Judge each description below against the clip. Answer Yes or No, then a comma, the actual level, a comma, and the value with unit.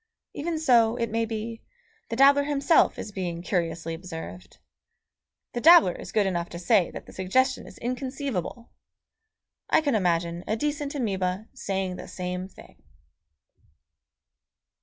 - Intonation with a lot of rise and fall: Yes, wide, 6.4 semitones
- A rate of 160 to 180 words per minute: No, average, 140 wpm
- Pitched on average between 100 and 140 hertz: No, high, 215 Hz